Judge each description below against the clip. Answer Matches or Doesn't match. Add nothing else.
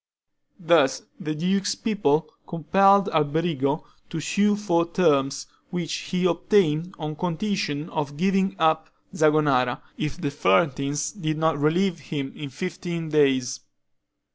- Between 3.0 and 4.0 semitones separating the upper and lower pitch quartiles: Matches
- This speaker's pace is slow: Matches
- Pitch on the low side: Doesn't match